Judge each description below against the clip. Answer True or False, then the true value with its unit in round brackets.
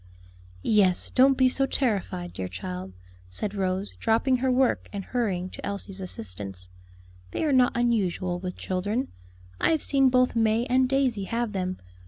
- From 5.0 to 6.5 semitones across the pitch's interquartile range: True (5.6 semitones)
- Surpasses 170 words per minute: False (160 wpm)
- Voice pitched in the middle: False (210 Hz)